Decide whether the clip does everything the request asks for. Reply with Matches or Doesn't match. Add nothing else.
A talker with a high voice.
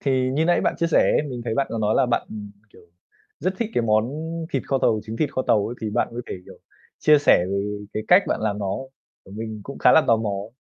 Doesn't match